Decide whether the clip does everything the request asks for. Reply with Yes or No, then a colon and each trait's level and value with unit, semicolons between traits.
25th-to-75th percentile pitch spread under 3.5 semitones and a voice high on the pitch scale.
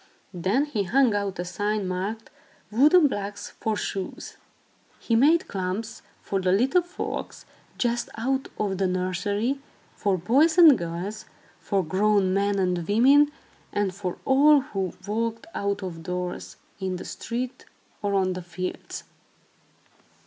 No: average, 4.6 semitones; high, 205 Hz